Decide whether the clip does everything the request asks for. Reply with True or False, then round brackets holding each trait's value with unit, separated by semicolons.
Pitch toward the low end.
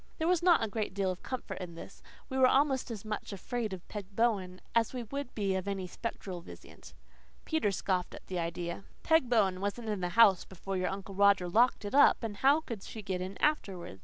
False (200 Hz)